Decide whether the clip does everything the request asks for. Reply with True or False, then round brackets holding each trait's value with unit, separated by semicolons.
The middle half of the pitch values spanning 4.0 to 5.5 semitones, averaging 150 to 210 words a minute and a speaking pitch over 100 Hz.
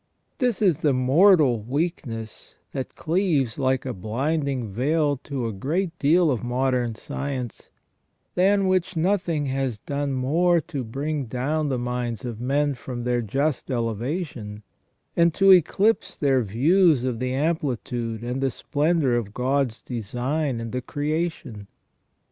False (4.5 semitones; 140 wpm; 135 Hz)